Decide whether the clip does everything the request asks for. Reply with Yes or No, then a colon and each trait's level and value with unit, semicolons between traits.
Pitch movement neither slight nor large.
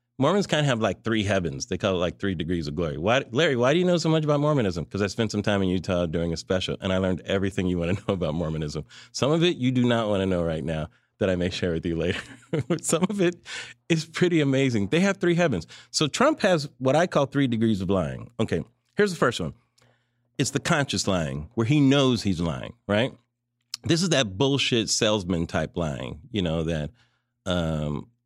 No: wide, 7.9 semitones